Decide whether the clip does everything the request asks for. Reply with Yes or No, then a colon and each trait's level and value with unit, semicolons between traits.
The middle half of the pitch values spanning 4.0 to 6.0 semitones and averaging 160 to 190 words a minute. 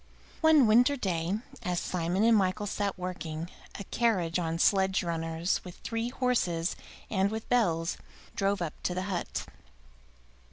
No: average, 4.3 semitones; average, 145 wpm